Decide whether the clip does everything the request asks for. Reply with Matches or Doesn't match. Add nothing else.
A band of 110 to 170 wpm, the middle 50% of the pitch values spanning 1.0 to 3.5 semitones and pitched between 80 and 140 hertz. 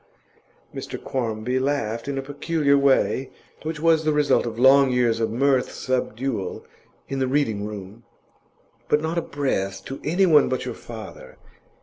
Doesn't match